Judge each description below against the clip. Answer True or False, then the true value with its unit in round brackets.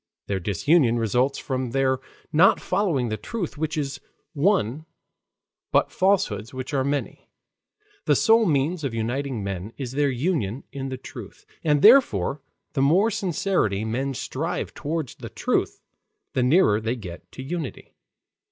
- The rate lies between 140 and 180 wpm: True (145 wpm)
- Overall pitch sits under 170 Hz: True (135 Hz)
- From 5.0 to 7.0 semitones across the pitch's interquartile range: True (5.6 semitones)